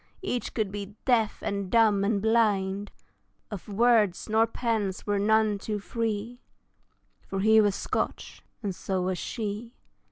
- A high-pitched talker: Yes, high, 210 Hz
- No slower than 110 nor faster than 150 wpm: Yes, average, 140 wpm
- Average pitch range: No, narrow, 2.0 semitones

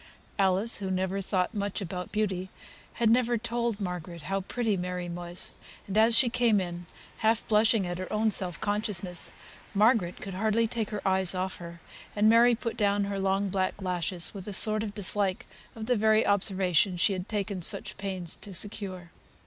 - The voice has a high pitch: Yes, high, 195 Hz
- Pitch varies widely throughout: No, average, 2.9 semitones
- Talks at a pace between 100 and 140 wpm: No, average, 180 wpm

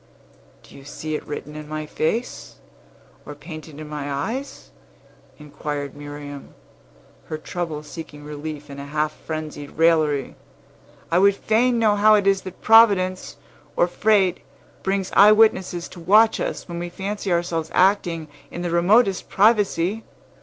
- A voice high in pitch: No, medium, 170 Hz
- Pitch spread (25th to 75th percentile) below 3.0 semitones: No, average, 4.9 semitones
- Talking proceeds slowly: No, average, 145 wpm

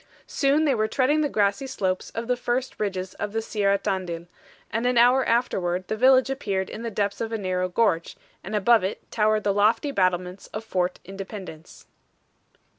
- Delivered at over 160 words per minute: Yes, average, 185 wpm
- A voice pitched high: Yes, high, 210 Hz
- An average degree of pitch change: Yes, average, 4.2 semitones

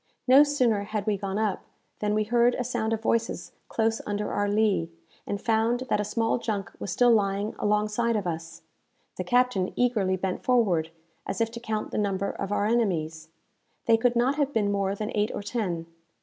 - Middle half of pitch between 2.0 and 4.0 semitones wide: Yes, average, 2.9 semitones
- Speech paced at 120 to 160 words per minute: No, average, 195 wpm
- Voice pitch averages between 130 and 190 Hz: No, high, 215 Hz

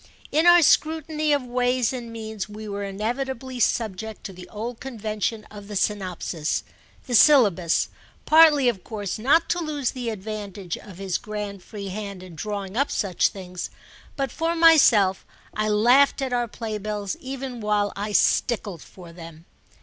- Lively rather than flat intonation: No, average, 4.4 semitones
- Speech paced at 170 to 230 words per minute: No, average, 155 wpm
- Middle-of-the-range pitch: No, high, 215 Hz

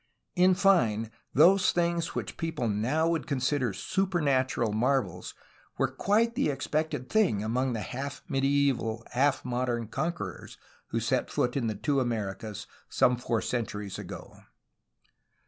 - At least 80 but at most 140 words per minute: Yes, slow, 135 wpm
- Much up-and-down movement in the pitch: Yes, wide, 5.8 semitones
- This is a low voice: Yes, low, 130 Hz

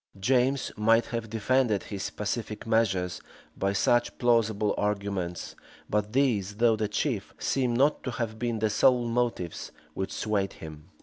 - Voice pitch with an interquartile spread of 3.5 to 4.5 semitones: No, average, 3.1 semitones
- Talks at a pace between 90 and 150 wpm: Yes, average, 145 wpm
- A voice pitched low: Yes, low, 110 Hz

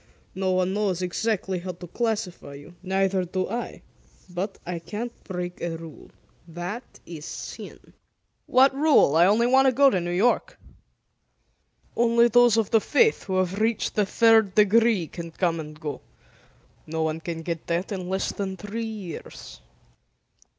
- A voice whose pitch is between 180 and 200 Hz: Yes, high, 190 Hz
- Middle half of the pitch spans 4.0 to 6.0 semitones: Yes, average, 4.5 semitones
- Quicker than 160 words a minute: No, average, 155 wpm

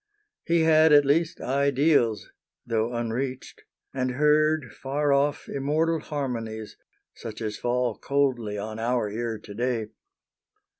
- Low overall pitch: Yes, low, 130 Hz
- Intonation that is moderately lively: Yes, average, 4.3 semitones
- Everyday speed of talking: No, slow, 120 wpm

